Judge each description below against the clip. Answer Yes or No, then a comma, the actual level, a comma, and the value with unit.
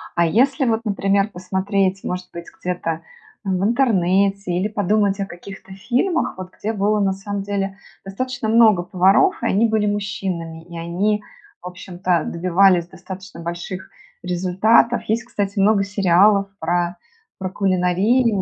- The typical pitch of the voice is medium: No, high, 195 Hz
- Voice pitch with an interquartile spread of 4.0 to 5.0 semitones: No, narrow, 2.6 semitones